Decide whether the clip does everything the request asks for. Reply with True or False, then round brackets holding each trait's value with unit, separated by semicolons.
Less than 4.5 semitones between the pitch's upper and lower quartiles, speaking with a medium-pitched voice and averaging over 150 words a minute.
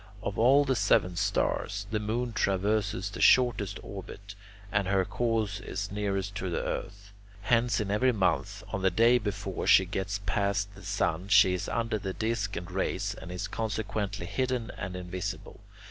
False (2.5 semitones; 100 Hz; 170 wpm)